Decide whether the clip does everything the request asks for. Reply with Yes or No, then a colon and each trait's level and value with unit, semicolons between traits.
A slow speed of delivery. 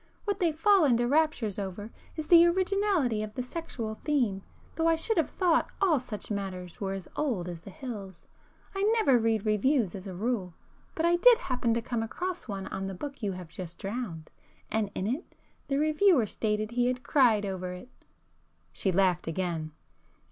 No: average, 185 wpm